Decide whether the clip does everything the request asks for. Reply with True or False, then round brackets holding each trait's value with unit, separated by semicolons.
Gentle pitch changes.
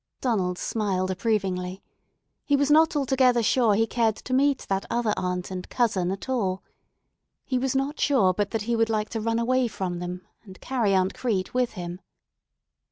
False (5.1 semitones)